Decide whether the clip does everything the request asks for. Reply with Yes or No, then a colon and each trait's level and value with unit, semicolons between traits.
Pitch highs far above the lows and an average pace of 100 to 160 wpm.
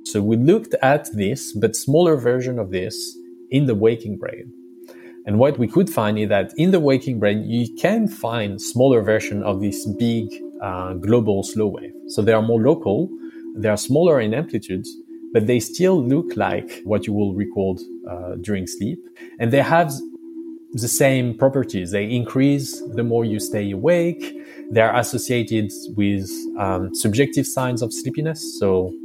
No: wide, 5.7 semitones; average, 170 wpm